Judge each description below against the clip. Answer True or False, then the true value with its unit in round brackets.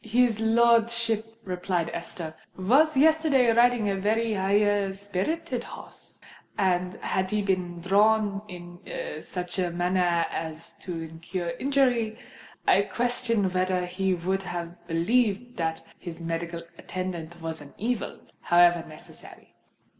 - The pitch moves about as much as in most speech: True (4.5 semitones)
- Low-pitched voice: False (190 Hz)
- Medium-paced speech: False (125 wpm)